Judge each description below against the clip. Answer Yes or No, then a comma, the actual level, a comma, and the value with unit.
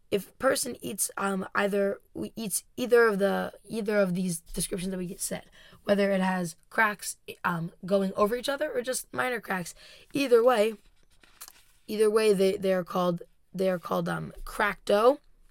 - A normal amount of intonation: Yes, average, 3.1 semitones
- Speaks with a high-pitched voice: Yes, high, 200 Hz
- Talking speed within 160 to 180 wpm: Yes, average, 175 wpm